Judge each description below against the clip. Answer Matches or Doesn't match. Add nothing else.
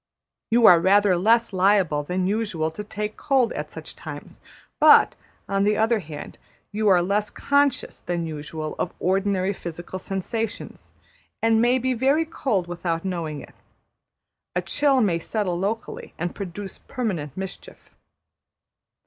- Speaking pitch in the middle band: Doesn't match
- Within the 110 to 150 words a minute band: Matches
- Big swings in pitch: Doesn't match